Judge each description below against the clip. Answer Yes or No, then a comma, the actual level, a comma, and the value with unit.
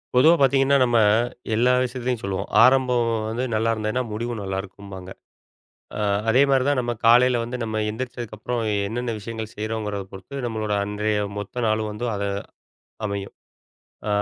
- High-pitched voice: No, low, 115 Hz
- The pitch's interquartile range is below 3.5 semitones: Yes, average, 2.9 semitones